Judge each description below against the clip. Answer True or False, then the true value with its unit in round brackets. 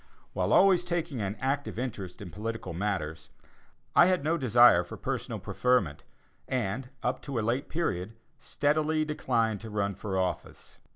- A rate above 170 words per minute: False (155 wpm)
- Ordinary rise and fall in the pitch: False (6.6 semitones)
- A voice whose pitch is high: False (115 Hz)